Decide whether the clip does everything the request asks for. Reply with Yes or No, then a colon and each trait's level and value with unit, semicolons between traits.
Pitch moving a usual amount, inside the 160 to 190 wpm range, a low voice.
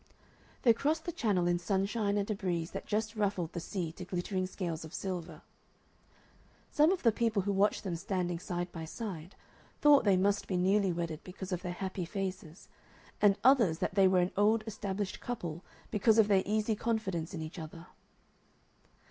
No: average, 3.1 semitones; average, 180 wpm; high, 190 Hz